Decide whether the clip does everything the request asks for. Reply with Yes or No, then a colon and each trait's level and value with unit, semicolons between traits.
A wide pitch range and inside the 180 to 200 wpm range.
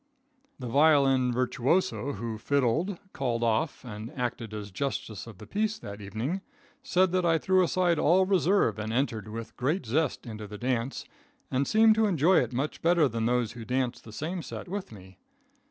Yes: wide, 7.1 semitones; average, 185 wpm